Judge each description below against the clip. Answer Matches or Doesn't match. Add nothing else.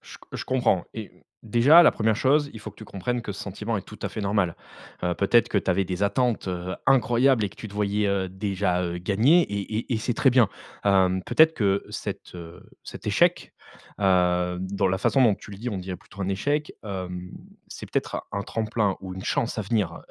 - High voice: Doesn't match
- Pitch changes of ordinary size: Matches